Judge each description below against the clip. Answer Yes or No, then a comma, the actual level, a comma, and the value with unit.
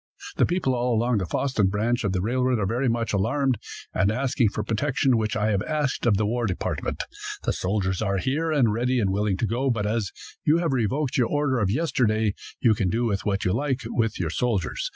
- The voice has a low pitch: Yes, low, 115 Hz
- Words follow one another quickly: Yes, fast, 215 wpm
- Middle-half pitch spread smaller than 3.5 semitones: No, average, 4.0 semitones